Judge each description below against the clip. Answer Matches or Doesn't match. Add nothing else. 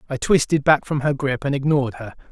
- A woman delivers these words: Doesn't match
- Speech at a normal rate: Doesn't match